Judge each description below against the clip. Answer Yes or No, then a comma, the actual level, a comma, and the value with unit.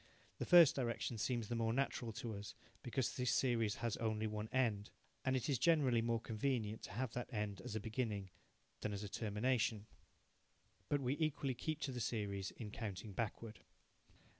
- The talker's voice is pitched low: Yes, low, 115 Hz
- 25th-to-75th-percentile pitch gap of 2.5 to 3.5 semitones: Yes, average, 3.2 semitones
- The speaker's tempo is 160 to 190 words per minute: Yes, average, 180 wpm